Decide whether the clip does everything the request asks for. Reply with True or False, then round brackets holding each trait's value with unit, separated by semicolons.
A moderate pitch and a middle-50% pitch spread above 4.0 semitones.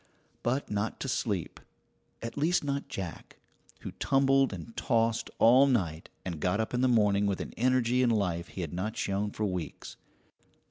False (110 Hz; 5.0 semitones)